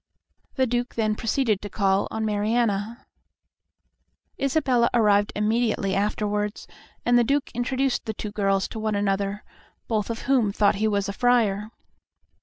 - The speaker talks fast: No, average, 145 wpm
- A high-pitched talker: Yes, high, 215 Hz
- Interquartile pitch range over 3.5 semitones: No, average, 2.9 semitones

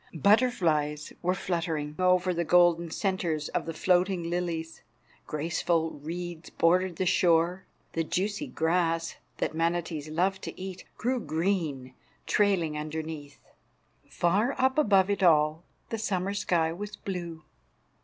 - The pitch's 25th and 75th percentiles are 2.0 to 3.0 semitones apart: Yes, average, 2.7 semitones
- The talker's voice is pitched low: No, medium, 170 Hz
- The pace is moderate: No, slow, 125 wpm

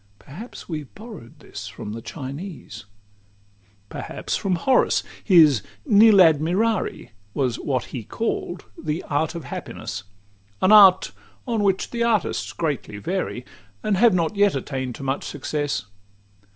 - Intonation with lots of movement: Yes, wide, 6.9 semitones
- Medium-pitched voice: Yes, medium, 165 Hz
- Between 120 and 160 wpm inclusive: Yes, average, 140 wpm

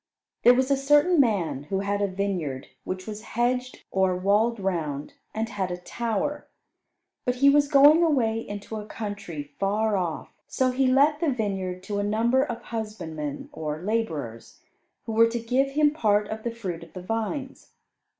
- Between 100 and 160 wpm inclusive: No, average, 175 wpm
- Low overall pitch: No, high, 220 Hz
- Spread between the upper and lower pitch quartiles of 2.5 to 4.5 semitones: No, average, 5.2 semitones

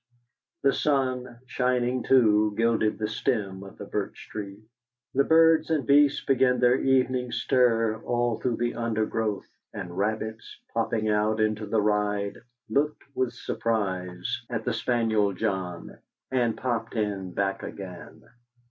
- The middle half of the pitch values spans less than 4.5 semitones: Yes, average, 3.2 semitones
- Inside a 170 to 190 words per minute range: No, slow, 135 wpm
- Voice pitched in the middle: No, low, 115 Hz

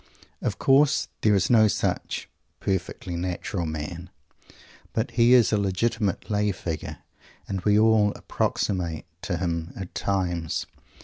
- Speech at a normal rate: No, slow, 130 wpm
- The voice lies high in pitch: No, very low, 95 Hz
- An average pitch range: Yes, average, 3.6 semitones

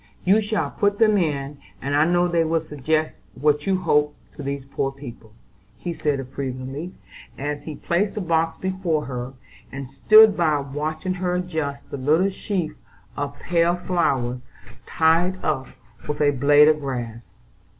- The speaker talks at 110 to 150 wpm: No, average, 160 wpm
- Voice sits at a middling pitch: Yes, medium, 155 Hz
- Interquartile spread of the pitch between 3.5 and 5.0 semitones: Yes, average, 4.1 semitones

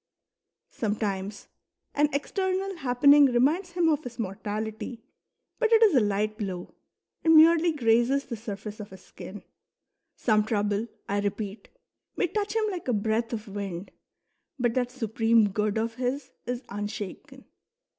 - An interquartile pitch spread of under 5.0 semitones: No, wide, 5.4 semitones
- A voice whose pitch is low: No, high, 230 Hz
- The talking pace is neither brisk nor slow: Yes, average, 145 wpm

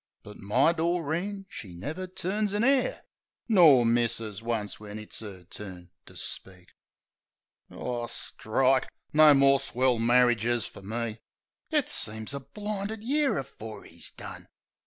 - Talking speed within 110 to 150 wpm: Yes, slow, 135 wpm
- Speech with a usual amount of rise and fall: No, wide, 8.1 semitones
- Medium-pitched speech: No, low, 125 Hz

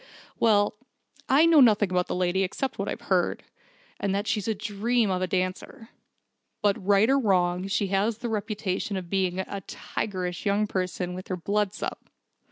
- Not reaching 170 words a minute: No, average, 175 wpm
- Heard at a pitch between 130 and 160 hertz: No, high, 200 Hz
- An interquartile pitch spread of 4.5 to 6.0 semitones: No, narrow, 2.6 semitones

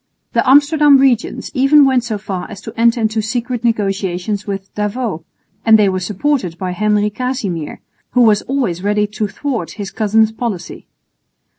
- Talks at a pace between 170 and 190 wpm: No, average, 160 wpm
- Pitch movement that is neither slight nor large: Yes, average, 4.0 semitones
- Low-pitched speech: No, high, 215 Hz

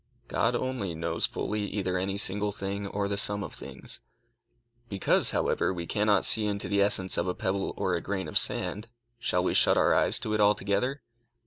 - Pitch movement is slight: Yes, narrow, 1.7 semitones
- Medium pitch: No, low, 100 Hz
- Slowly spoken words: No, average, 195 wpm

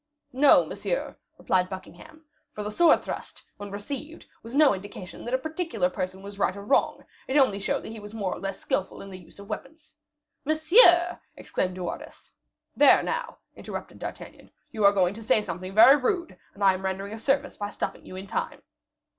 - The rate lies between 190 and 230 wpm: Yes, average, 200 wpm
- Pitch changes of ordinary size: No, wide, 7.0 semitones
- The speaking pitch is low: No, high, 210 Hz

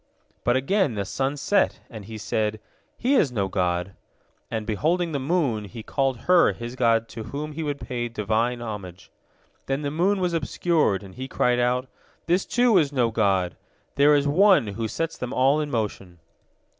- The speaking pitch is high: No, low, 125 Hz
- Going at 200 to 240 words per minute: No, average, 180 wpm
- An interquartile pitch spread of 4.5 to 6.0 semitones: Yes, wide, 5.6 semitones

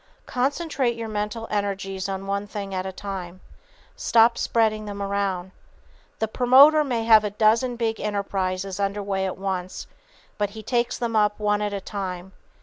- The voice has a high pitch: Yes, high, 205 Hz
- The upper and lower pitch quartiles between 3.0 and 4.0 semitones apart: No, narrow, 2.6 semitones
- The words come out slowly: No, average, 165 wpm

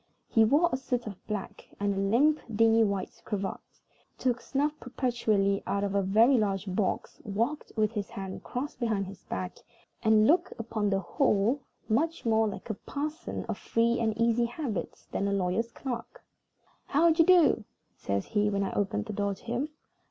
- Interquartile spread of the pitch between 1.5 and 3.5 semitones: No, average, 3.9 semitones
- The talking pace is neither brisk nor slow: Yes, average, 180 wpm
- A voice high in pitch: Yes, high, 220 Hz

